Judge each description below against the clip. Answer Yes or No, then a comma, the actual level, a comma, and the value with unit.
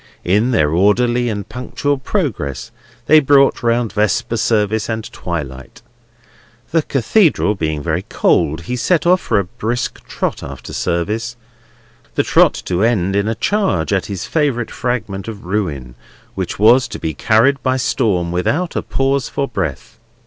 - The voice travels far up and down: Yes, wide, 6.0 semitones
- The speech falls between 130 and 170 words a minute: Yes, average, 155 wpm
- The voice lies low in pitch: Yes, low, 110 Hz